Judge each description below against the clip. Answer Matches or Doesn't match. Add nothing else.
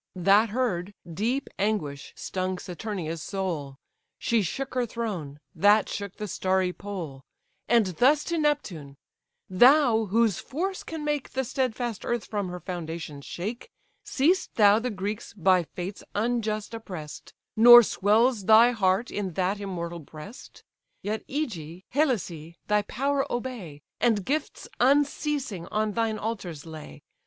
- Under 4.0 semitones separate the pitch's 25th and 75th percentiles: Doesn't match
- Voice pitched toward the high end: Matches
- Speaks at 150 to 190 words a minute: Doesn't match